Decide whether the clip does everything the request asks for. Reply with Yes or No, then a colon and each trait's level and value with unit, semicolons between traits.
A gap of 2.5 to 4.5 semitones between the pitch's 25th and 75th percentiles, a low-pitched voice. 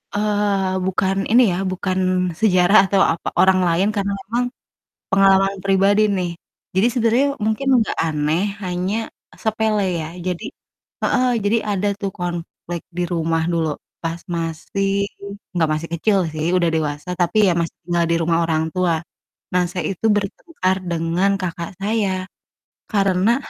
No: average, 3.1 semitones; medium, 185 Hz